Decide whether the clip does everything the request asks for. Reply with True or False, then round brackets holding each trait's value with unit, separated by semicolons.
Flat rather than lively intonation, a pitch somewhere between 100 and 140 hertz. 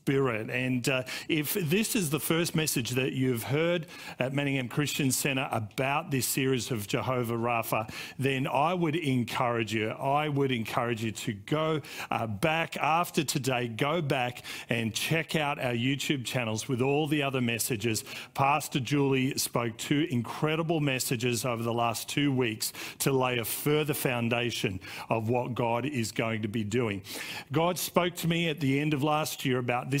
False (4.0 semitones; 135 Hz)